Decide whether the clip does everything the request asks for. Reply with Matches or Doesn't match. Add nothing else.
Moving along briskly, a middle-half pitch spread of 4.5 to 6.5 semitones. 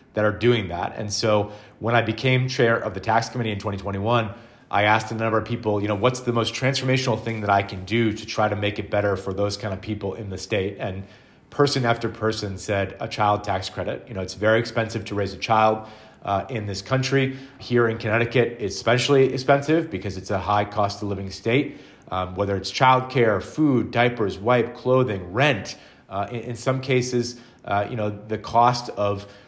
Doesn't match